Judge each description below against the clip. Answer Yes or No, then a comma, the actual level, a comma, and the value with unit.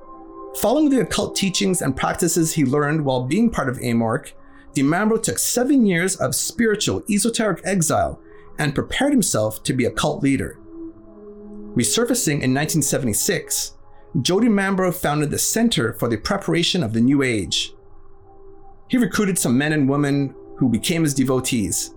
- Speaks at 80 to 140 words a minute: No, average, 150 wpm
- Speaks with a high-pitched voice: No, medium, 170 Hz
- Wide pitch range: Yes, wide, 7.8 semitones